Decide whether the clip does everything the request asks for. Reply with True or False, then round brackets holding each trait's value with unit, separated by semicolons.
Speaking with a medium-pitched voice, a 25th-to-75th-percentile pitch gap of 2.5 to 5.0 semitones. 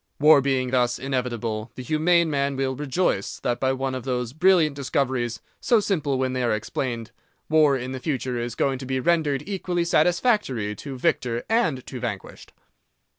False (130 Hz; 3.8 semitones)